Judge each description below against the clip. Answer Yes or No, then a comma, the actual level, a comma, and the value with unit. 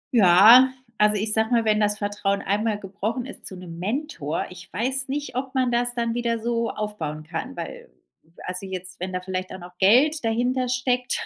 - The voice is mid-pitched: No, high, 215 Hz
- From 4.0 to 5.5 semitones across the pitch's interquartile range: Yes, average, 4.7 semitones